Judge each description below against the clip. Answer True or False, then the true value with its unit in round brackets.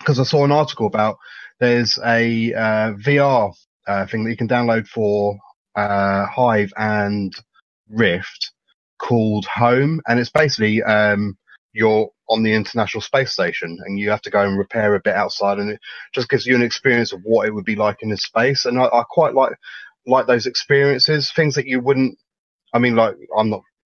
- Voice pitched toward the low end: True (110 Hz)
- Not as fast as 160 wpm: False (190 wpm)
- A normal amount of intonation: True (3.0 semitones)